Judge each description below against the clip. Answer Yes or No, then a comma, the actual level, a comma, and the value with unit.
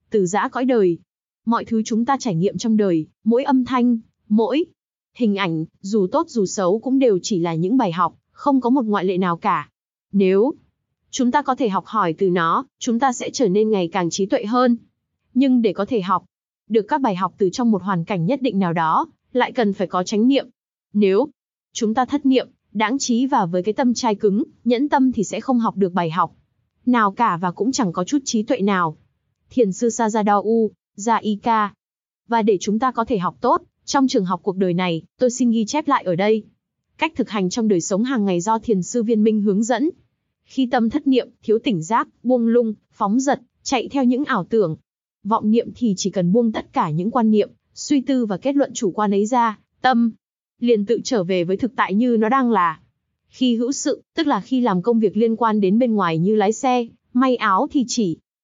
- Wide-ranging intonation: No, average, 4.2 semitones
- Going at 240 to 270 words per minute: No, average, 225 wpm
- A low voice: No, high, 225 Hz